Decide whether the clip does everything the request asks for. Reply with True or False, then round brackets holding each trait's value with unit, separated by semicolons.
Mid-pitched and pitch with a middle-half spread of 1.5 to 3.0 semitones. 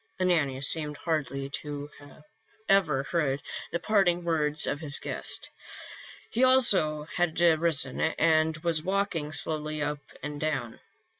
True (155 Hz; 2.7 semitones)